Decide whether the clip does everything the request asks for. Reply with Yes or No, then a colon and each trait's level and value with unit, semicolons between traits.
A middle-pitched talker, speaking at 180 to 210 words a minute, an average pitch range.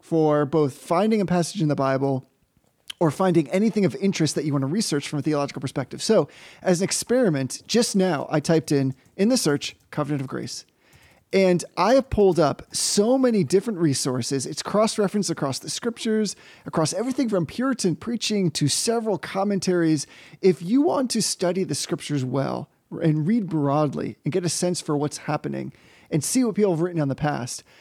No: medium, 170 Hz; average, 185 wpm; wide, 5.7 semitones